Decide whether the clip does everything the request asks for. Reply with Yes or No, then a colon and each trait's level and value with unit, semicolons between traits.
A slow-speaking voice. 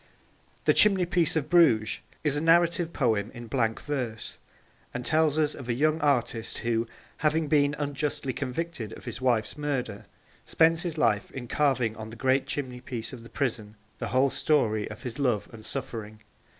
No: average, 170 wpm